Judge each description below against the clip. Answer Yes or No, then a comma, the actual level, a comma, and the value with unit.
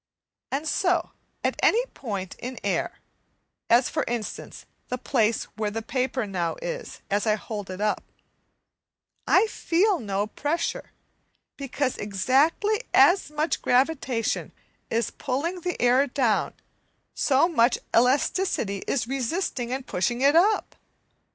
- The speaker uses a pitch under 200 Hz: No, very high, 255 Hz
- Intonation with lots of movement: Yes, wide, 6.2 semitones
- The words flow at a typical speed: No, slow, 130 wpm